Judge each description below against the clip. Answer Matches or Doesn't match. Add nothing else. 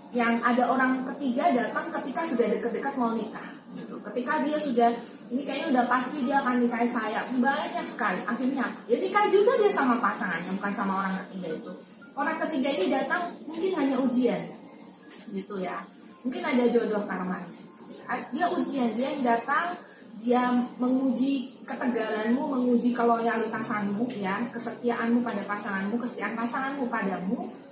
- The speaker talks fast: Matches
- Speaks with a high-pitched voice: Matches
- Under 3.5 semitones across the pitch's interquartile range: Matches